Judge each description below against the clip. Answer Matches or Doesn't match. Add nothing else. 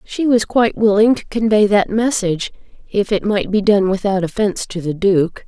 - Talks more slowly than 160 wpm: Doesn't match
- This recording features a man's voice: Doesn't match